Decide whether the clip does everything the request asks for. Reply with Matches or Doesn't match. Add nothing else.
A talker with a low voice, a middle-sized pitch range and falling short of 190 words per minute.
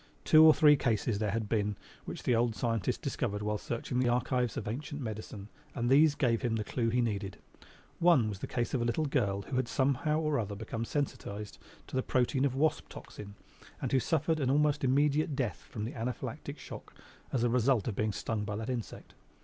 Doesn't match